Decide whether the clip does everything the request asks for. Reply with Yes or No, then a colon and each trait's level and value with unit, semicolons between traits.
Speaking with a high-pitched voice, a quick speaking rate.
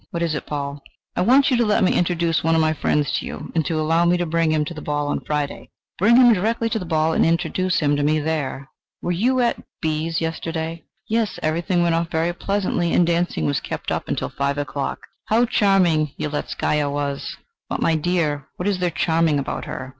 No: medium, 165 Hz; fast, 220 wpm